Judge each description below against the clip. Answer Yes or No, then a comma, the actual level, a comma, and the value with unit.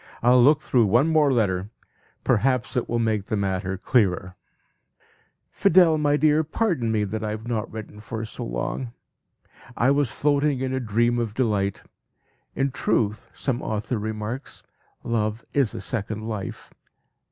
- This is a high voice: No, low, 115 Hz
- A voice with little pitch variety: No, average, 3.9 semitones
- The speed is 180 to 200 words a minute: No, average, 150 wpm